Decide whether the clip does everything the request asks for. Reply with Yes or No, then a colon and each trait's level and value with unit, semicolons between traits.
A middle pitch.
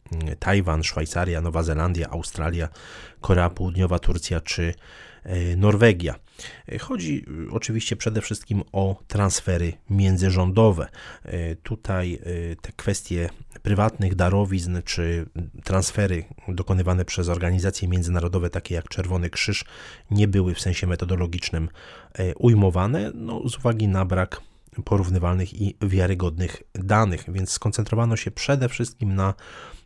No: very low, 95 Hz